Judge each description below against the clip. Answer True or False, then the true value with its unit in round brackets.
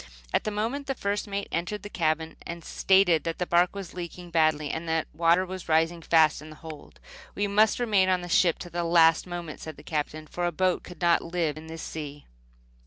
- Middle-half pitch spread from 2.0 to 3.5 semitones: True (2.7 semitones)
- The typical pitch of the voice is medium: True (170 Hz)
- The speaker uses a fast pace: True (220 wpm)